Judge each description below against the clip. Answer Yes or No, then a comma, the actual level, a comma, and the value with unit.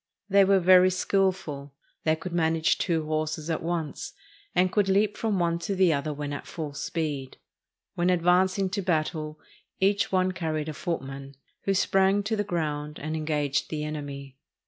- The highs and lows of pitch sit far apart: No, average, 3.6 semitones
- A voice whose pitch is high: No, medium, 165 Hz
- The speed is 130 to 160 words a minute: No, average, 170 wpm